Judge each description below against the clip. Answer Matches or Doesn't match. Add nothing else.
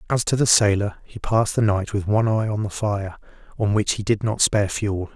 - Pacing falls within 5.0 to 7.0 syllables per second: Matches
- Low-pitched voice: Matches